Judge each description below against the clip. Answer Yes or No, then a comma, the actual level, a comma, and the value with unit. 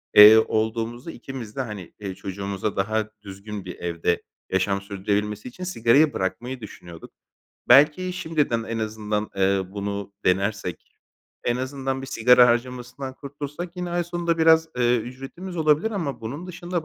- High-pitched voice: No, low, 120 Hz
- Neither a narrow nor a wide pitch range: No, wide, 6.2 semitones